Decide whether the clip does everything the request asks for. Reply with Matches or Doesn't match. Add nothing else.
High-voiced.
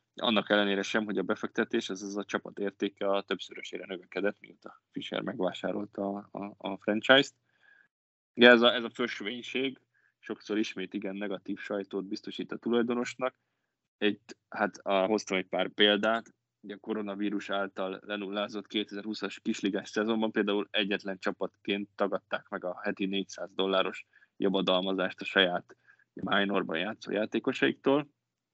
Doesn't match